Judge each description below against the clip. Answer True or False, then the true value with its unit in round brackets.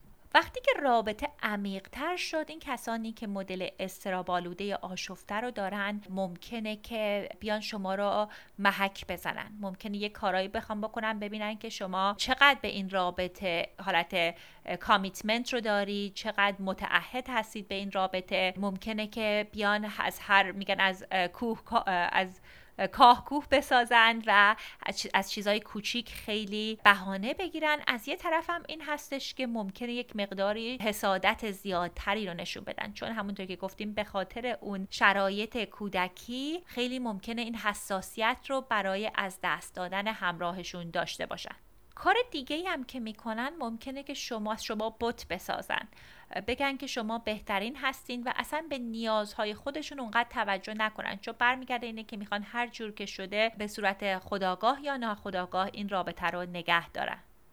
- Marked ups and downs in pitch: False (3.6 semitones)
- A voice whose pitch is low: False (210 Hz)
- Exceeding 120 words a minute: True (150 wpm)